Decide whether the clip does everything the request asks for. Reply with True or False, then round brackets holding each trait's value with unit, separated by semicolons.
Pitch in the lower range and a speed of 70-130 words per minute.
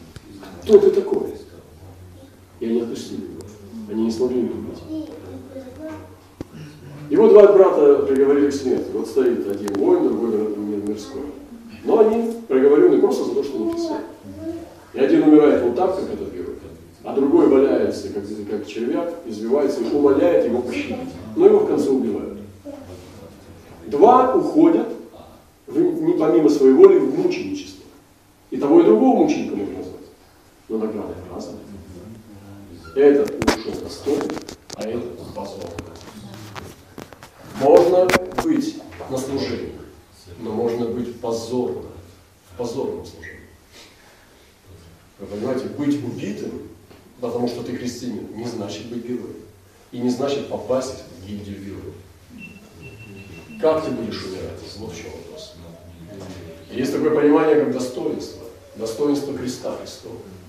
True (125 Hz; 125 wpm)